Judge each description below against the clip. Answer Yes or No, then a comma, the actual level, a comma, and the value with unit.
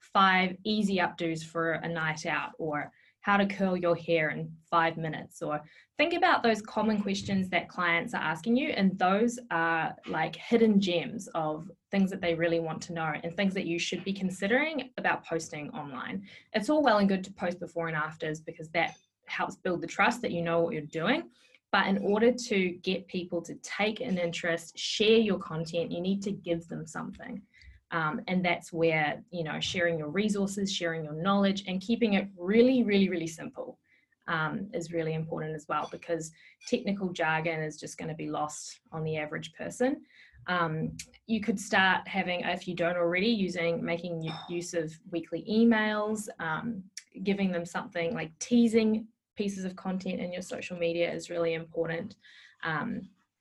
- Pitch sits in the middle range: Yes, medium, 180 Hz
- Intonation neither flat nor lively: Yes, average, 3.8 semitones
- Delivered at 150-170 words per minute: No, average, 180 wpm